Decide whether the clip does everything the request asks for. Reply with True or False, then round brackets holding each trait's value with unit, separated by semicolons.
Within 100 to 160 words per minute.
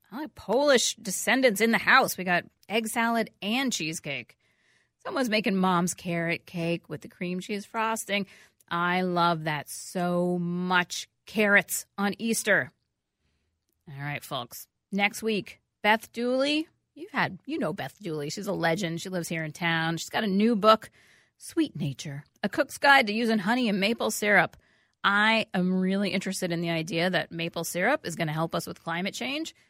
False (170 wpm)